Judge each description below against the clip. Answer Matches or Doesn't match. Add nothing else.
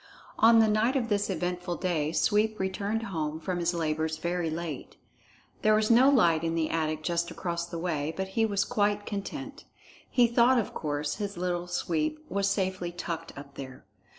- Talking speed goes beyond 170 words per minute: Matches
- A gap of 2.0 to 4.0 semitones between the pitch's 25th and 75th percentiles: Doesn't match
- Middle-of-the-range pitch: Matches